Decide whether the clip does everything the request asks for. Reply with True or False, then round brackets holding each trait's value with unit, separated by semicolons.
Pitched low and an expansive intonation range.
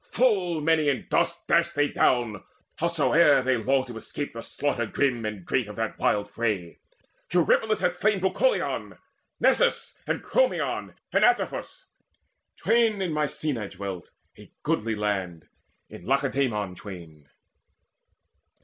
True (130 Hz; 8.3 semitones)